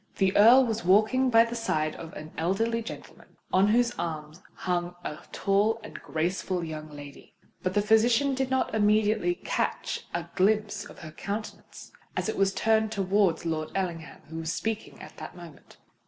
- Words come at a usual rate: Yes, average, 170 wpm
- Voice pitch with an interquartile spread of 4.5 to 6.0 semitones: Yes, average, 4.9 semitones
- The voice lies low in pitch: No, high, 200 Hz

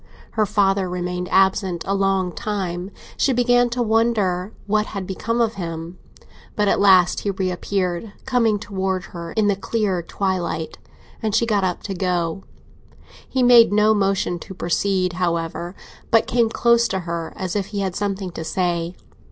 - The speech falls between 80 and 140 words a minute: No, average, 170 wpm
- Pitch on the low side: No, high, 195 Hz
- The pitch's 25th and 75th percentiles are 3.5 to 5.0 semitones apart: No, average, 3.0 semitones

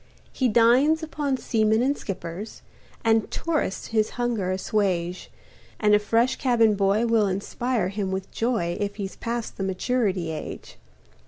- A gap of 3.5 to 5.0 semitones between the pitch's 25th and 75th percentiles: Yes, average, 3.8 semitones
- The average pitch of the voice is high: Yes, high, 215 Hz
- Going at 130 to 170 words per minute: Yes, average, 145 wpm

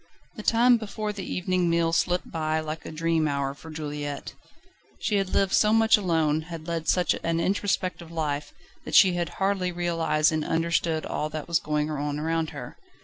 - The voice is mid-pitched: Yes, medium, 165 Hz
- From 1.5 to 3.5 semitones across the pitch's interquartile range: Yes, average, 3.0 semitones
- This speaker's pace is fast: No, average, 185 wpm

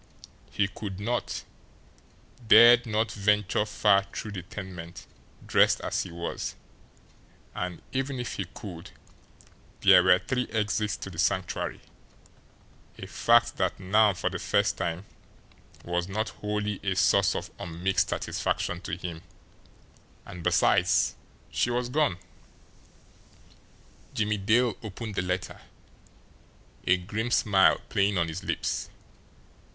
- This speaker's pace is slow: Yes, slow, 125 wpm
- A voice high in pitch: No, low, 100 Hz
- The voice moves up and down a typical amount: Yes, average, 3.3 semitones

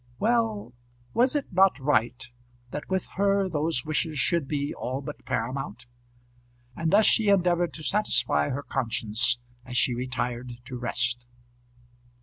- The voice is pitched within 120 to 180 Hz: Yes, medium, 140 Hz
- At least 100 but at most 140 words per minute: Yes, slow, 135 wpm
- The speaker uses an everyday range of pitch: No, wide, 6.9 semitones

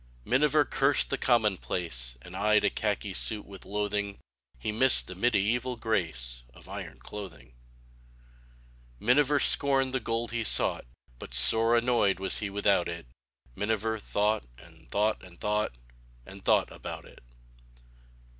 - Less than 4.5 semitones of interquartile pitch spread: Yes, average, 3.7 semitones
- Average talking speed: Yes, average, 145 wpm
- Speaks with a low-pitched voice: Yes, low, 105 Hz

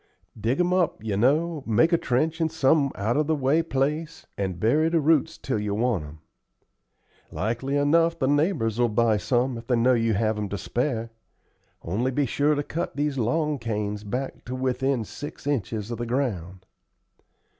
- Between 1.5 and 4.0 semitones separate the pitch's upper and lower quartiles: No, average, 5.0 semitones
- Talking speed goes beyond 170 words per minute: Yes, average, 185 wpm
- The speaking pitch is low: Yes, low, 130 Hz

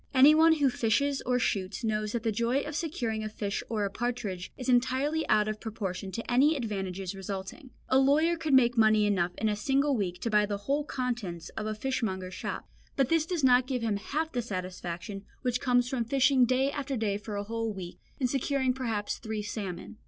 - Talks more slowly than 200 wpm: No, fast, 205 wpm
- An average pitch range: Yes, average, 4.5 semitones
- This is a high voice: Yes, high, 230 Hz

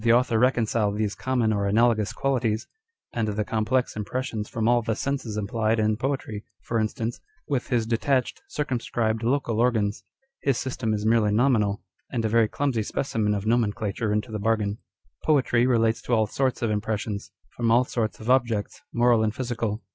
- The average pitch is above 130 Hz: No, low, 115 Hz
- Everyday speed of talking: Yes, average, 170 wpm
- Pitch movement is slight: Yes, narrow, 2.3 semitones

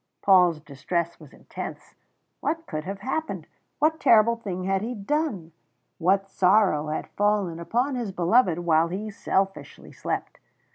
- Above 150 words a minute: No, average, 140 wpm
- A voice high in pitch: Yes, high, 195 Hz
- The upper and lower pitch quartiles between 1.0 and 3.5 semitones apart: No, average, 5.0 semitones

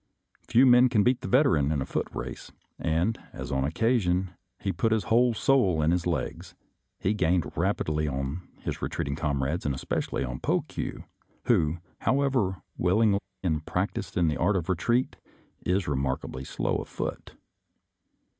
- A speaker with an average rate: Yes, average, 170 wpm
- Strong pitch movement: Yes, wide, 6.9 semitones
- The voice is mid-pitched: No, very low, 90 Hz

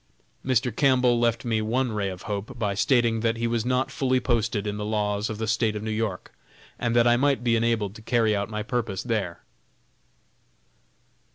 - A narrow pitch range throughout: Yes, narrow, 2.3 semitones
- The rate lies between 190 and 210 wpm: Yes, average, 195 wpm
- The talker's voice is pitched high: No, low, 115 Hz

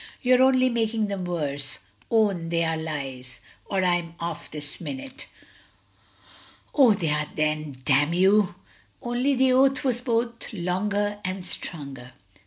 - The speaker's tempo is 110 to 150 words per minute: Yes, slow, 135 wpm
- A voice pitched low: No, medium, 185 Hz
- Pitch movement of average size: No, wide, 7.4 semitones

